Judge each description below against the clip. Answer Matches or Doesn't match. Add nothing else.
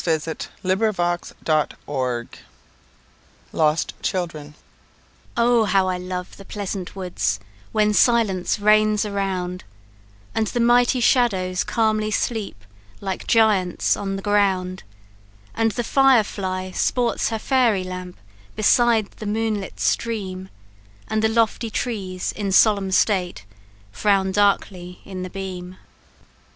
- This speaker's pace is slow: Matches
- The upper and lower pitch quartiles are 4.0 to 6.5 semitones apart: Doesn't match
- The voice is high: Matches